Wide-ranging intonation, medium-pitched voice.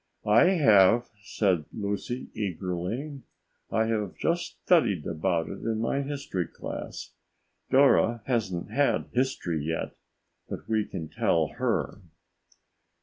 No: wide, 6.1 semitones; low, 110 Hz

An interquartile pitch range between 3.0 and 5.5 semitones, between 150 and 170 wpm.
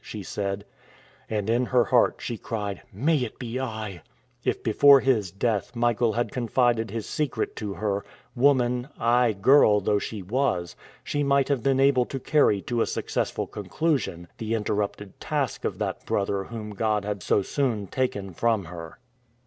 Yes: average, 3.9 semitones; average, 165 wpm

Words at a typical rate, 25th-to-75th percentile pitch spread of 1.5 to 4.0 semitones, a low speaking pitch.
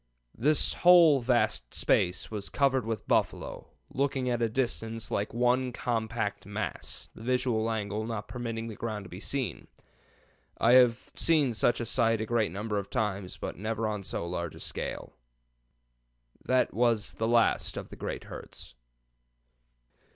Yes: average, 155 wpm; average, 2.9 semitones; low, 115 Hz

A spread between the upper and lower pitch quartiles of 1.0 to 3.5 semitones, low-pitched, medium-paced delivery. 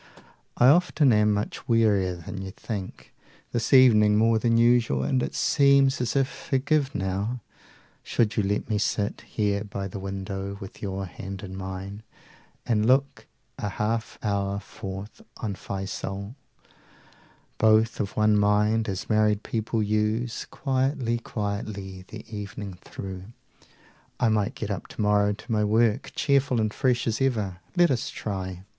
Yes: average, 3.0 semitones; low, 105 Hz; average, 150 wpm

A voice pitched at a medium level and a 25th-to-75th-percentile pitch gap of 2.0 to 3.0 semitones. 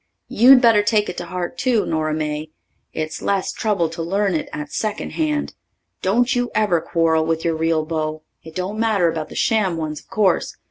No: medium, 175 Hz; average, 5.1 semitones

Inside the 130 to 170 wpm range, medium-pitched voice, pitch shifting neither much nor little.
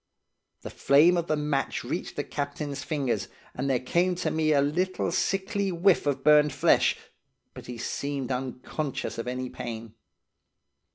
Yes: average, 155 wpm; medium, 145 Hz; average, 4.6 semitones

